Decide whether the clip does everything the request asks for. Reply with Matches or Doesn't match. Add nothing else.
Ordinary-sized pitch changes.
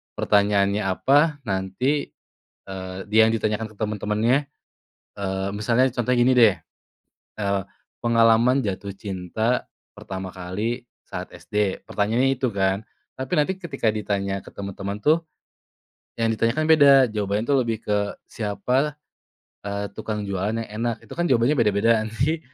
Matches